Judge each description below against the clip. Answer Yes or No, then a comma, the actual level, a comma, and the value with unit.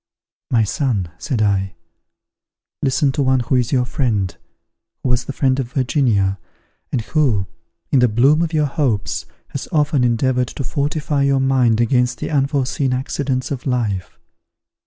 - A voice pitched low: Yes, low, 130 Hz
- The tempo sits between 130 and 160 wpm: Yes, average, 155 wpm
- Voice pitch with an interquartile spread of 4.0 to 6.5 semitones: No, average, 3.0 semitones